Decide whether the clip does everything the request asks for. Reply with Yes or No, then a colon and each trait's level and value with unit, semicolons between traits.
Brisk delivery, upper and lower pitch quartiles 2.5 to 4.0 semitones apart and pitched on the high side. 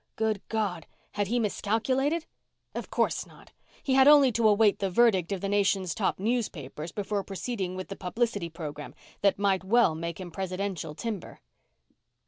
No: average, 160 wpm; average, 3.7 semitones; high, 200 Hz